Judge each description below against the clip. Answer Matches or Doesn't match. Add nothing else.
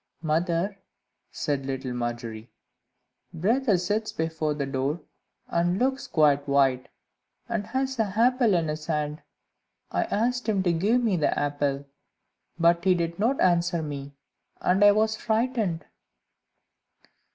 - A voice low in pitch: Doesn't match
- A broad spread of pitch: Matches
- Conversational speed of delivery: Doesn't match